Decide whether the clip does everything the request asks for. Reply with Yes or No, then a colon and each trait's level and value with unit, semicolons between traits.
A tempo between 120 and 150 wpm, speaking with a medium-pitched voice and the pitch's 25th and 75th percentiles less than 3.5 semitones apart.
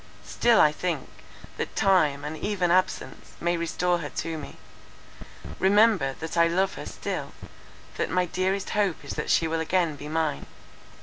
No: average, 165 wpm; medium, 170 Hz; average, 2.9 semitones